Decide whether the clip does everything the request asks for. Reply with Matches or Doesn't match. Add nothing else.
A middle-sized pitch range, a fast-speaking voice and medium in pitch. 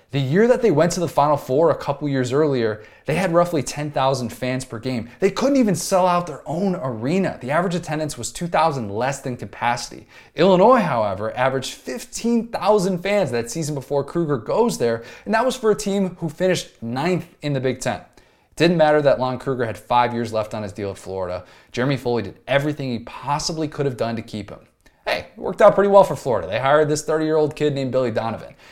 Doesn't match